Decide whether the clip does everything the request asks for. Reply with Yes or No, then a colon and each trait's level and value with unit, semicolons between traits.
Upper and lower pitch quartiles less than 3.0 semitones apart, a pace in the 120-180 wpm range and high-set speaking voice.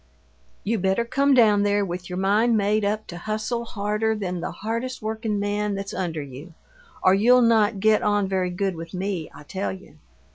No: narrow, 2.5 semitones; average, 190 wpm; high, 205 Hz